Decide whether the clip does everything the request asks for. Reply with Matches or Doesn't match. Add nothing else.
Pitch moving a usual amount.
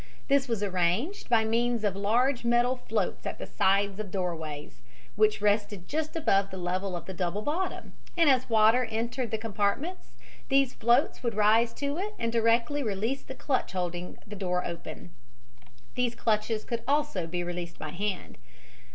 Matches